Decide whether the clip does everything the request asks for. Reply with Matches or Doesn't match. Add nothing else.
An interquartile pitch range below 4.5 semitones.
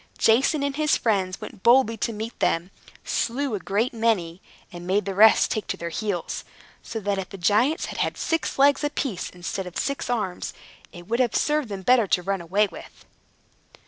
Doesn't match